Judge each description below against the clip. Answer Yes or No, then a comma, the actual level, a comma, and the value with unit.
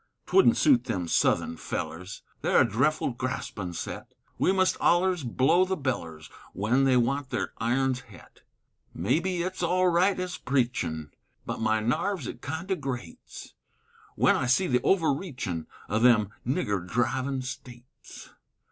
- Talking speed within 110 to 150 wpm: Yes, average, 145 wpm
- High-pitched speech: No, low, 130 Hz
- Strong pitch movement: Yes, wide, 7.5 semitones